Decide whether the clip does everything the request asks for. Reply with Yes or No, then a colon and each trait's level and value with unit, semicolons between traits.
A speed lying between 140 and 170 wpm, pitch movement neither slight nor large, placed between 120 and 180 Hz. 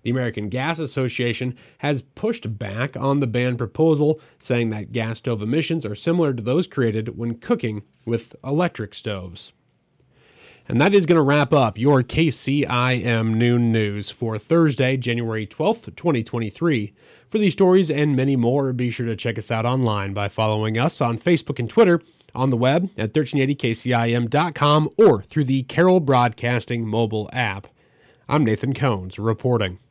Yes: average, 155 wpm; average, 4.6 semitones; low, 125 Hz